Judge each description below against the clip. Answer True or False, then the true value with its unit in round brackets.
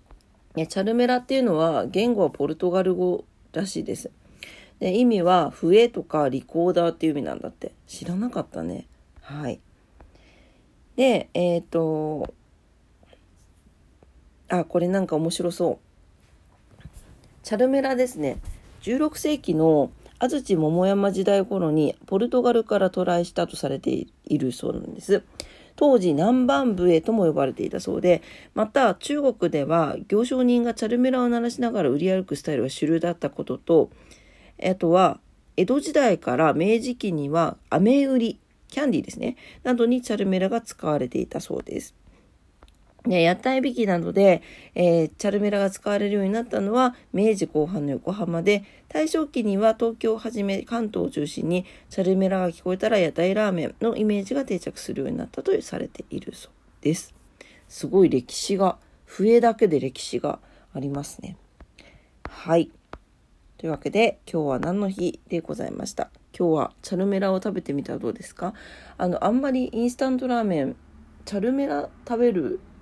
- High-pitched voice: True (195 Hz)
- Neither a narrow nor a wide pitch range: False (6.0 semitones)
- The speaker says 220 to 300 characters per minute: False (320 characters per minute)